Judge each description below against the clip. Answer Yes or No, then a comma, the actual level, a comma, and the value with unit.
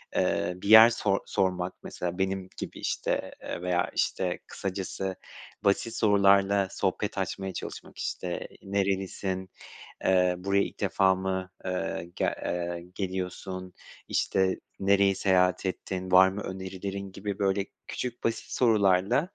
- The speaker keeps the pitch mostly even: Yes, narrow, 1.3 semitones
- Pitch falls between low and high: No, very low, 95 Hz